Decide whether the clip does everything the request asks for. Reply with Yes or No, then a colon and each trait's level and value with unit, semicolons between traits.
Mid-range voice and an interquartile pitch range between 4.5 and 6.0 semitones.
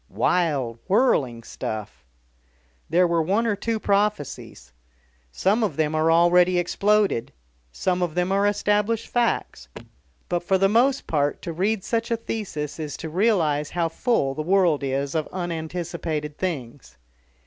Yes: medium, 175 Hz; average, 5.2 semitones